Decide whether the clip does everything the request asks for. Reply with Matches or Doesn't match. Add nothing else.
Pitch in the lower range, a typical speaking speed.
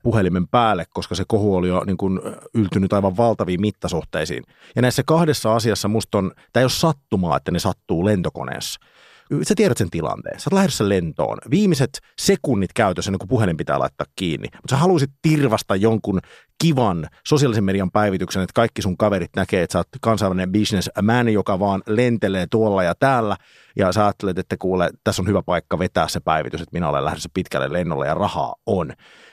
Doesn't match